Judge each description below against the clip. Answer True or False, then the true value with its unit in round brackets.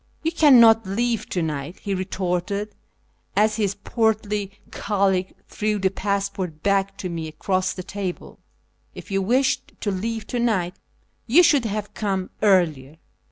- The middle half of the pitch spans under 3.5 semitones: True (2.9 semitones)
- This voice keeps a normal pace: True (155 wpm)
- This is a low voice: False (200 Hz)